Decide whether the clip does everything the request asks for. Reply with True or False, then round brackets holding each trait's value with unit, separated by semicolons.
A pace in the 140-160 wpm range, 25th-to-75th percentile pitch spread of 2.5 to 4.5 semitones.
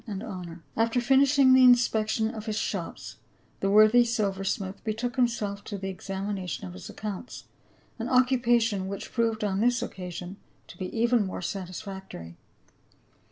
True (145 wpm; 3.8 semitones)